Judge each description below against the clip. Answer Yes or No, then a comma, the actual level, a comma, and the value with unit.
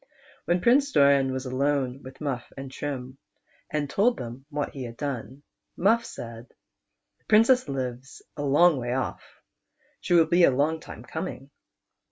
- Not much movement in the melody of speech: No, average, 3.9 semitones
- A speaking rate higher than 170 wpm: No, average, 165 wpm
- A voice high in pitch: No, medium, 140 Hz